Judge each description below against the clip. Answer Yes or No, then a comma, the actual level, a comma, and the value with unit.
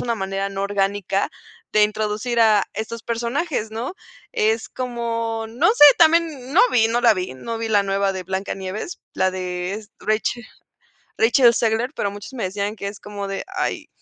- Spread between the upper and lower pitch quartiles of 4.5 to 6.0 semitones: No, average, 2.9 semitones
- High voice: Yes, high, 220 Hz